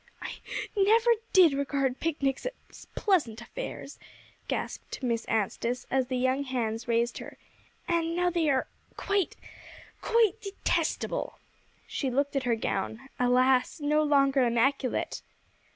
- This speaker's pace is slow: Yes, slow, 125 wpm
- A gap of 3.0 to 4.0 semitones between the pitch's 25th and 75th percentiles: No, average, 4.9 semitones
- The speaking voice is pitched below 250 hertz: No, very high, 275 Hz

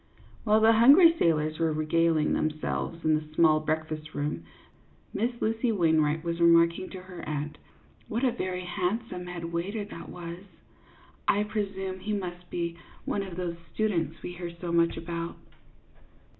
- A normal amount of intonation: Yes, average, 3.6 semitones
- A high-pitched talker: No, medium, 170 Hz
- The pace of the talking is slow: No, average, 155 wpm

